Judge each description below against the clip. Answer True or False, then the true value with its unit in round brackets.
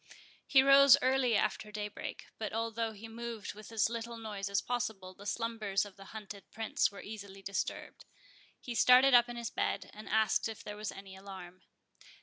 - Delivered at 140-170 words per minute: False (185 wpm)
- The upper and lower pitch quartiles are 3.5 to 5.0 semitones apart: False (2.7 semitones)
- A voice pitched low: False (220 Hz)